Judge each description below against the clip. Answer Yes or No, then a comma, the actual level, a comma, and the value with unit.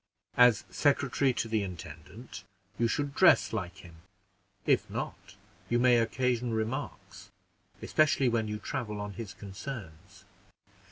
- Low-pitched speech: Yes, low, 115 Hz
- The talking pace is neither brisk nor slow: No, slow, 125 wpm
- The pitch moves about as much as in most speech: Yes, average, 3.8 semitones